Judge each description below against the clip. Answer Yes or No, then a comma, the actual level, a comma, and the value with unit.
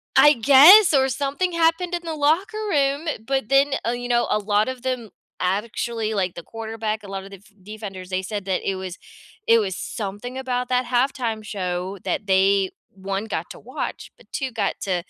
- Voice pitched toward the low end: No, high, 225 Hz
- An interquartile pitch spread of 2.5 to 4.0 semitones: No, wide, 5.4 semitones